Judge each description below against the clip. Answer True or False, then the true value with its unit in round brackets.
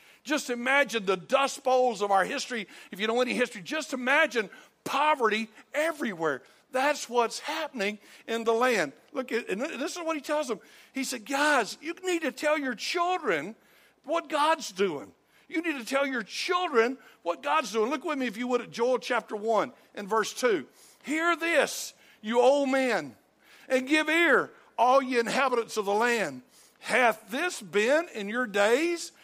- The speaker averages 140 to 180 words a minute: True (175 wpm)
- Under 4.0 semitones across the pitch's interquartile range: False (5.1 semitones)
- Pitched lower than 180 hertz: False (260 Hz)